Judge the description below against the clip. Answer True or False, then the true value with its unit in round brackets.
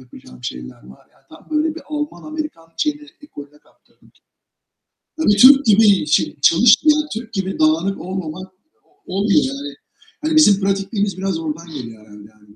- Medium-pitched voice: False (195 Hz)